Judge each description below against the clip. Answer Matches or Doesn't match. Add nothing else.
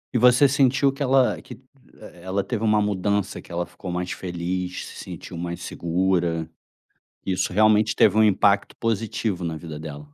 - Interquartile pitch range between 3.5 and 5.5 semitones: Matches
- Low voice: Matches